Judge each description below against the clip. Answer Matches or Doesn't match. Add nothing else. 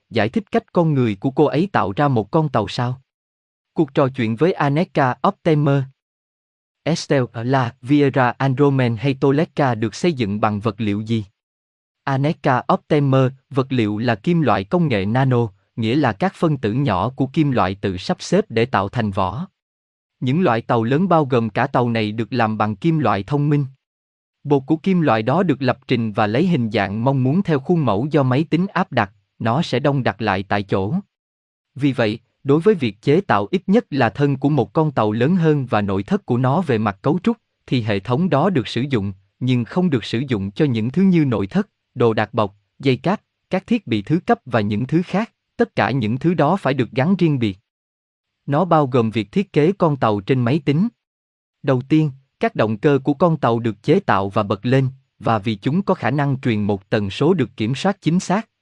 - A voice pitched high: Doesn't match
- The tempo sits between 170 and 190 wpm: Doesn't match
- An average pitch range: Doesn't match